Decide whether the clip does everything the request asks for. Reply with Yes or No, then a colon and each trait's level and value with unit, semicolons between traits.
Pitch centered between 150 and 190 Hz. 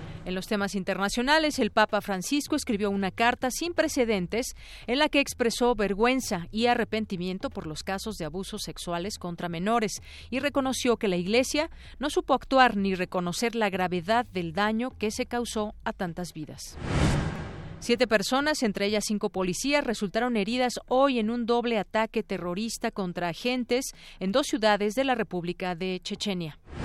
No: high, 220 Hz